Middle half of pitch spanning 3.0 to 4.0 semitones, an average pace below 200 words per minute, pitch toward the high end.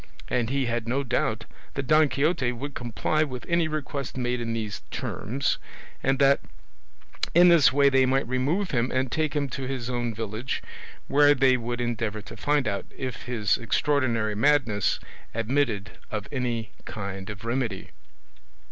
No: average, 3.6 semitones; average, 160 wpm; low, 125 Hz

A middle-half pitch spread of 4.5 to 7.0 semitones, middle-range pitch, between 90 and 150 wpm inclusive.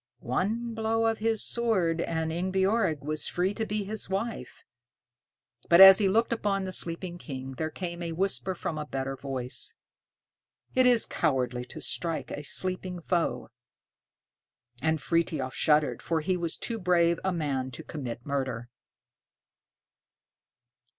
Yes: average, 4.8 semitones; medium, 170 Hz; average, 145 wpm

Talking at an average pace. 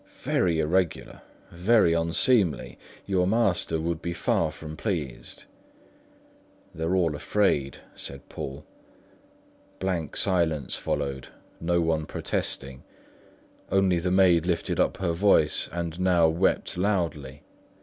No: slow, 110 wpm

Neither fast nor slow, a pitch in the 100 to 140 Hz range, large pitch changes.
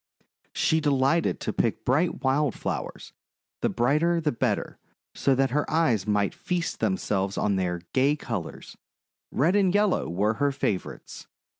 Yes: average, 155 wpm; low, 135 Hz; wide, 7.2 semitones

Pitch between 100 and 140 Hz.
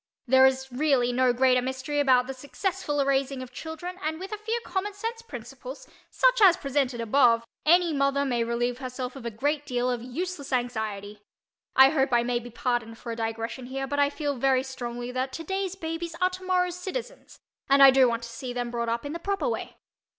No: very high, 265 Hz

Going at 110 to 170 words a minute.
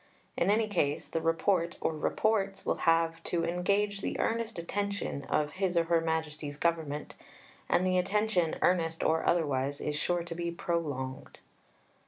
Yes: average, 155 wpm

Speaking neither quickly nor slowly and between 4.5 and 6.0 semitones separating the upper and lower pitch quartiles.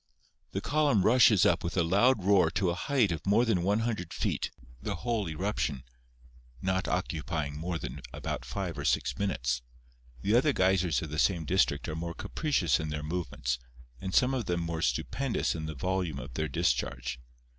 Yes: average, 180 wpm; average, 4.9 semitones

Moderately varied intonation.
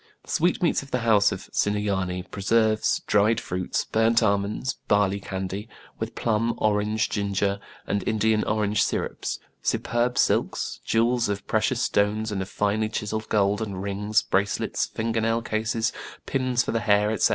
No: narrow, 2.0 semitones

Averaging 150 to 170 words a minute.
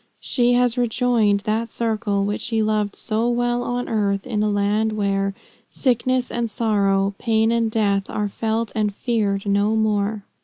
Yes: average, 160 wpm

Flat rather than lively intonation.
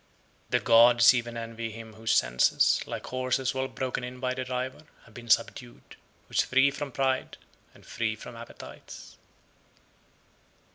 Yes: narrow, 2.1 semitones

